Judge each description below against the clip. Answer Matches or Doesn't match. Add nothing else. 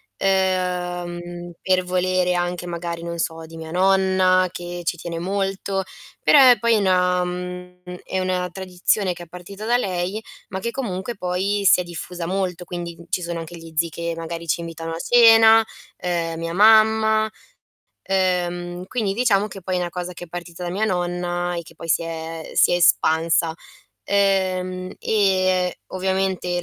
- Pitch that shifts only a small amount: Matches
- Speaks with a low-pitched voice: Doesn't match